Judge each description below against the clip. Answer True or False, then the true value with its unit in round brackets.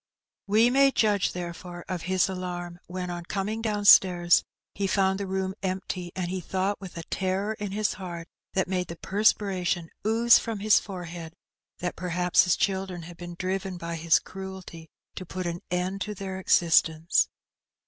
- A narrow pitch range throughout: True (2.0 semitones)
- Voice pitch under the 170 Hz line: False (185 Hz)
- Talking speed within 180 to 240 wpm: False (170 wpm)